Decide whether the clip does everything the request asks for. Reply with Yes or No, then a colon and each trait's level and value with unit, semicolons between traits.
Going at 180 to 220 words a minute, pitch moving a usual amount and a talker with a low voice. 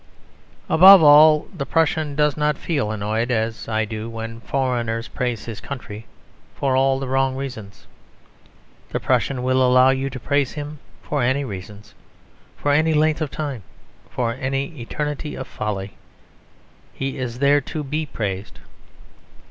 No: average, 150 wpm; average, 4.2 semitones; low, 130 Hz